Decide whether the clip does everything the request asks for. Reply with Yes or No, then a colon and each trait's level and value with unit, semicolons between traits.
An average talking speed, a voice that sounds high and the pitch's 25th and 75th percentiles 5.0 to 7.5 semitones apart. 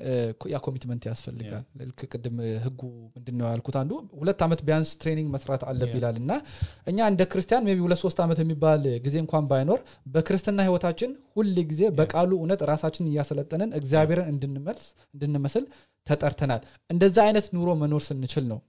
No: average, 145 wpm; medium, 150 Hz; average, 5.3 semitones